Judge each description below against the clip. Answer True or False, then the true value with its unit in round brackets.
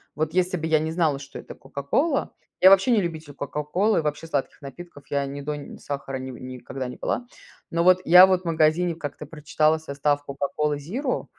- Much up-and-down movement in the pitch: False (3.8 semitones)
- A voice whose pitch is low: False (155 Hz)